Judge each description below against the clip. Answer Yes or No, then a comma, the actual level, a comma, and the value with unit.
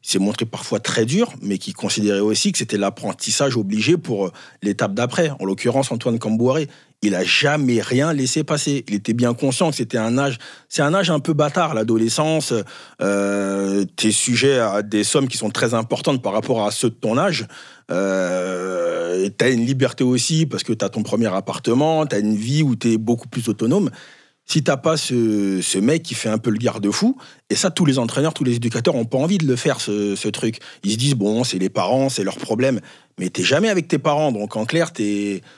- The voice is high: No, low, 120 Hz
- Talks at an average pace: No, fast, 225 wpm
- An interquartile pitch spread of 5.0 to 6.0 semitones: Yes, wide, 5.5 semitones